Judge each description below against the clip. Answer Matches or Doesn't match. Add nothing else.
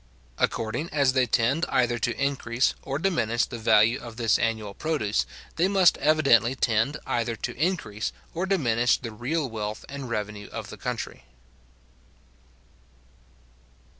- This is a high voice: Doesn't match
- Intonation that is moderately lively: Matches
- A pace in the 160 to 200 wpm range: Doesn't match